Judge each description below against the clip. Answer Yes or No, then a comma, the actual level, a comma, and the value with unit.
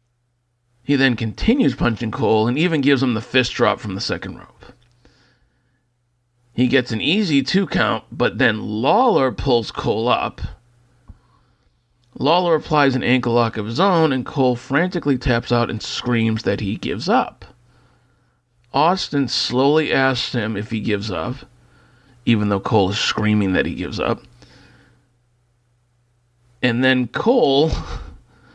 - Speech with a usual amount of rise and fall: No, narrow, 1.8 semitones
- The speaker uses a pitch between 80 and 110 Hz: No, low, 120 Hz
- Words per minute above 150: No, average, 140 wpm